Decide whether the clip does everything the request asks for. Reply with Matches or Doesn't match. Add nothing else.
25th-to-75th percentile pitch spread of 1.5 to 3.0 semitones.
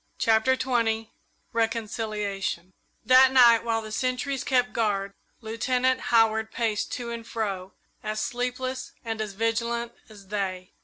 Matches